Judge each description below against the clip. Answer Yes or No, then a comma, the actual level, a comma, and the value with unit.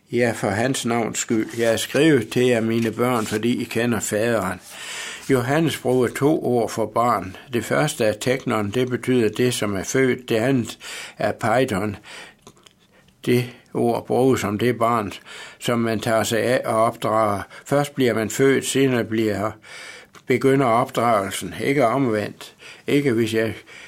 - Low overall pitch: Yes, low, 115 Hz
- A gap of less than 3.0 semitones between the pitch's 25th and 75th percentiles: Yes, narrow, 2.5 semitones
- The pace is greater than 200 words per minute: No, average, 155 wpm